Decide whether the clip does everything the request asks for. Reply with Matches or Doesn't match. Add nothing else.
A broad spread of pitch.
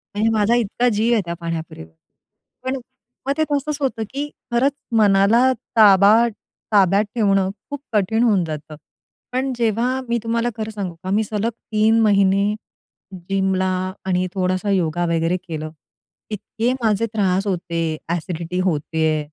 Doesn't match